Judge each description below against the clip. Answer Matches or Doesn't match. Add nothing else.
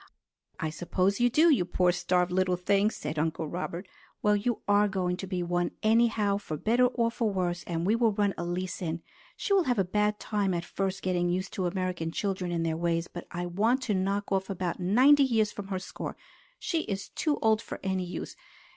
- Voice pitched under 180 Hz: Doesn't match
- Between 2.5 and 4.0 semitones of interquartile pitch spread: Matches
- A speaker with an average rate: Doesn't match